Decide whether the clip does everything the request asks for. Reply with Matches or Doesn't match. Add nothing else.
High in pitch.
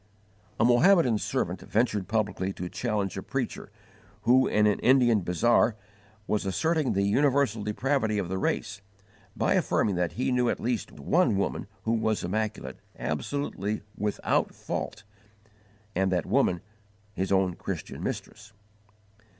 Doesn't match